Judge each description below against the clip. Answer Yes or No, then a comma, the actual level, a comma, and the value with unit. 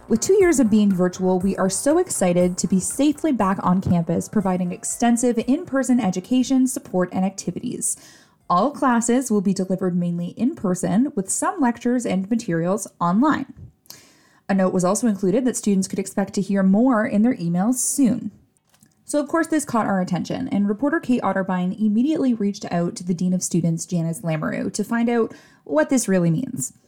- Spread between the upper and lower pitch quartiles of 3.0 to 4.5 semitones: No, average, 5.3 semitones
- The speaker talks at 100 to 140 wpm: No, average, 185 wpm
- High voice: Yes, high, 210 Hz